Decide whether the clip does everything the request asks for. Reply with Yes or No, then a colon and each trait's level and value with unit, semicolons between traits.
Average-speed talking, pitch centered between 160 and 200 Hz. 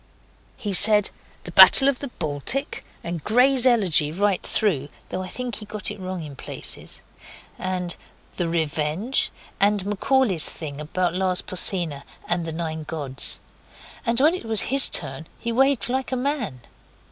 Yes: average, 155 wpm; high, 190 Hz